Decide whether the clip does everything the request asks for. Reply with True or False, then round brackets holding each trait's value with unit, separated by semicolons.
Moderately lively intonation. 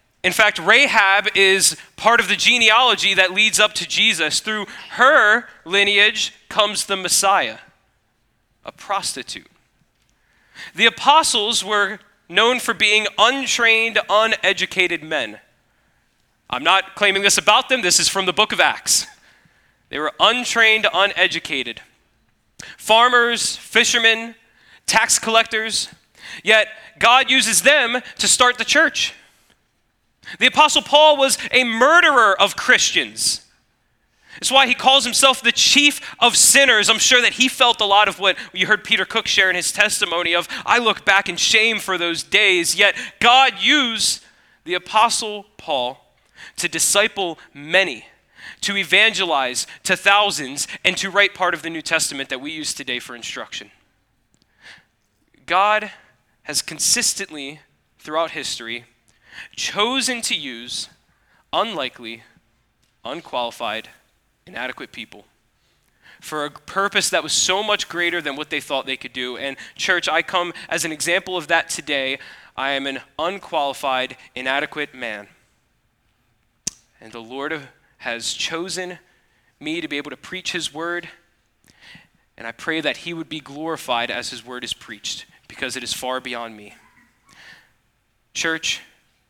False (6.2 semitones)